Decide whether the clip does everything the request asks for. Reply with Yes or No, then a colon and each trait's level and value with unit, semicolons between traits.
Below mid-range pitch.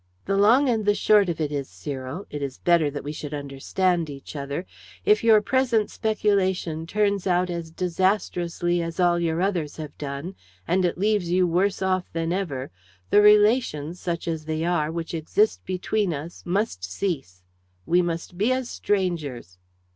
No: medium, 175 Hz